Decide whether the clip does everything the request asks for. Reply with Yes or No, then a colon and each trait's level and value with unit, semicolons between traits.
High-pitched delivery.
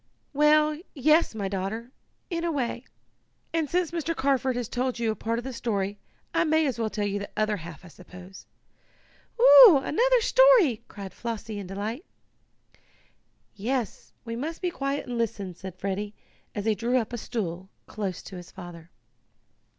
Yes: high, 230 Hz